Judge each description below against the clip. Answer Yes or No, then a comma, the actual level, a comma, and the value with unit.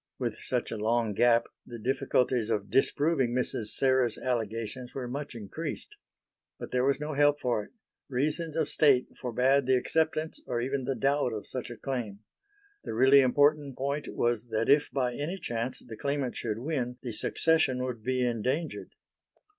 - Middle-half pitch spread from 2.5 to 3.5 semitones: Yes, average, 3.1 semitones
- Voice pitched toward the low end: Yes, low, 130 Hz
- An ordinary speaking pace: Yes, average, 170 wpm